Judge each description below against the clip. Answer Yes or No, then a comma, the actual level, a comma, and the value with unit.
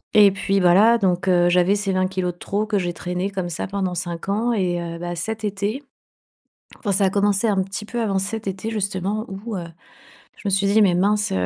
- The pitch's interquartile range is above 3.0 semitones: No, narrow, 2.4 semitones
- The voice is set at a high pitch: Yes, high, 195 Hz